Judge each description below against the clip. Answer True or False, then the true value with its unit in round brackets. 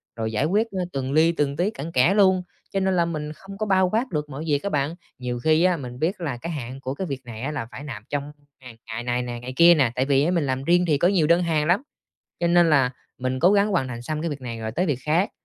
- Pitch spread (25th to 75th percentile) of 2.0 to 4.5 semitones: False (5.2 semitones)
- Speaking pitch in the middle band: True (150 Hz)